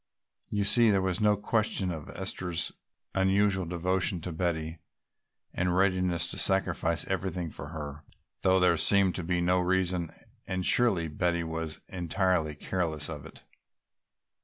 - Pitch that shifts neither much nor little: No, narrow, 2.3 semitones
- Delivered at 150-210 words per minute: No, average, 140 wpm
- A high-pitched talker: No, very low, 90 Hz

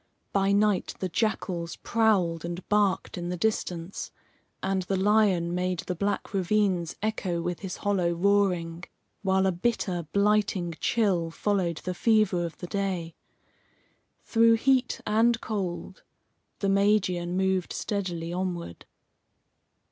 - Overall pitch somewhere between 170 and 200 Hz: Yes, high, 190 Hz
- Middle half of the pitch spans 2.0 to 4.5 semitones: Yes, average, 3.0 semitones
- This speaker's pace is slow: Yes, slow, 125 wpm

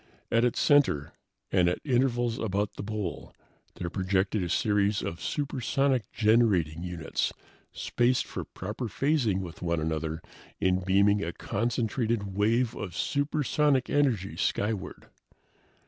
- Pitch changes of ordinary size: Yes, average, 4.8 semitones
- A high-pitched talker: No, low, 105 Hz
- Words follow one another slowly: Yes, slow, 125 wpm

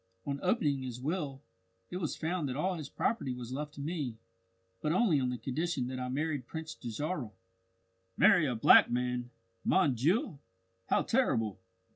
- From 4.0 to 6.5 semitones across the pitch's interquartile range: Yes, average, 4.5 semitones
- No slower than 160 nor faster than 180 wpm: Yes, average, 165 wpm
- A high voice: No, medium, 140 Hz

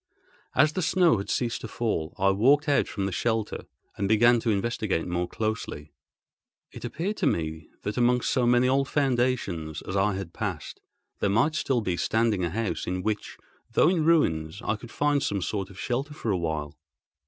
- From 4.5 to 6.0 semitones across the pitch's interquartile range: Yes, average, 5.1 semitones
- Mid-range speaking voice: No, low, 110 Hz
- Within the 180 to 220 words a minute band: Yes, average, 190 wpm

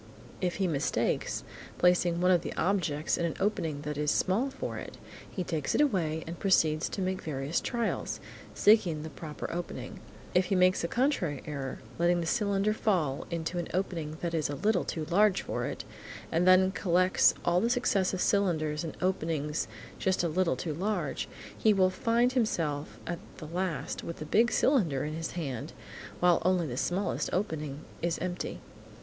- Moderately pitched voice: Yes, medium, 175 Hz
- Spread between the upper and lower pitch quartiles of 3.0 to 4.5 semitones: Yes, average, 3.5 semitones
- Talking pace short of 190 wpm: Yes, average, 180 wpm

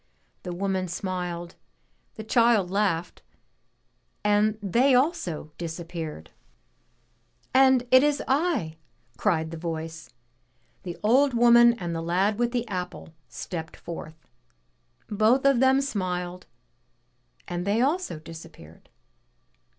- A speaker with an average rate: No, slow, 95 wpm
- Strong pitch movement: Yes, wide, 6.1 semitones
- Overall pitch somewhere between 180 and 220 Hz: Yes, high, 190 Hz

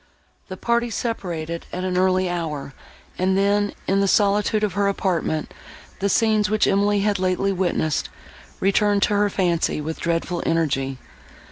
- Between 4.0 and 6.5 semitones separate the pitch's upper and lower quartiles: No, average, 3.2 semitones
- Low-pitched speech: No, high, 190 Hz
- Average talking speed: Yes, average, 150 wpm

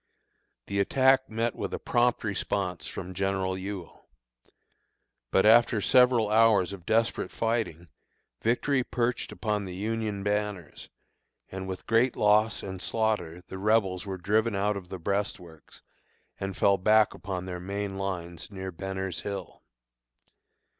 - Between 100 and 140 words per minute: Yes, slow, 135 wpm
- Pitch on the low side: Yes, low, 100 Hz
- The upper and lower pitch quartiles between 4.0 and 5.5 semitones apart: No, average, 2.8 semitones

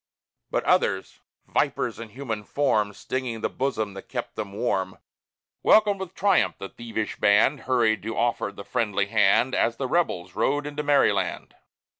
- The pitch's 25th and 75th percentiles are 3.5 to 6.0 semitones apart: Yes, average, 5.1 semitones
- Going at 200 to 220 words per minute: No, average, 155 wpm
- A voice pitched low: Yes, low, 115 Hz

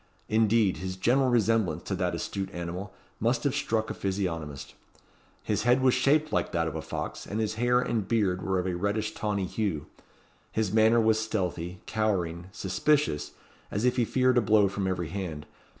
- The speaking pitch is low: Yes, low, 105 Hz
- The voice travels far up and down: No, average, 3.9 semitones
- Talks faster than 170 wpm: Yes, average, 180 wpm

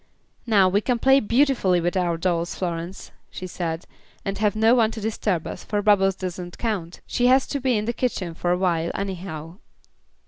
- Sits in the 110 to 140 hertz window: No, high, 195 Hz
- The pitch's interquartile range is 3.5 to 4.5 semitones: Yes, average, 4.0 semitones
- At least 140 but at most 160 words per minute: No, average, 195 wpm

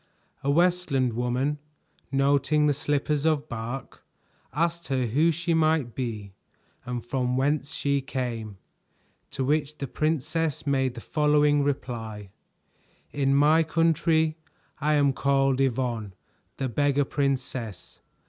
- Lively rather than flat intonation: No, average, 3.1 semitones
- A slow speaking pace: Yes, slow, 120 wpm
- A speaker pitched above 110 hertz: Yes, medium, 140 Hz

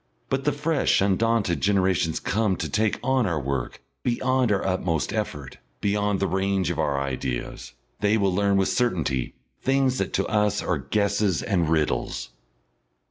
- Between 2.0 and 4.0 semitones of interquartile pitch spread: No, average, 4.8 semitones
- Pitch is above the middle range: No, low, 100 Hz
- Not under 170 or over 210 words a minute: No, average, 155 wpm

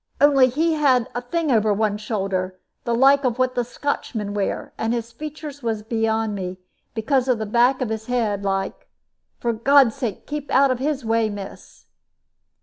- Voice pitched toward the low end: No, high, 235 Hz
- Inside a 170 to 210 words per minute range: Yes, average, 180 wpm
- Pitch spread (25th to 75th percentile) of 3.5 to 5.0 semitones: Yes, average, 3.8 semitones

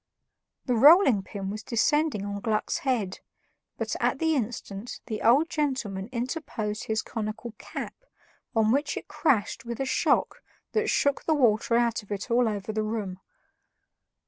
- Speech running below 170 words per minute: Yes, average, 155 wpm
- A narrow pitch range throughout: No, average, 4.1 semitones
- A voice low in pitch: No, high, 230 Hz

